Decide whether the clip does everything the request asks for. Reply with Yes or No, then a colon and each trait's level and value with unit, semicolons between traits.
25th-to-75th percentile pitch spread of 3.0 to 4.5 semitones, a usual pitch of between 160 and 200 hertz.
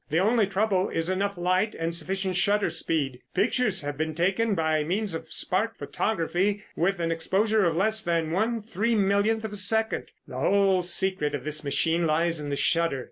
Yes: average, 4.0 semitones; medium, 185 Hz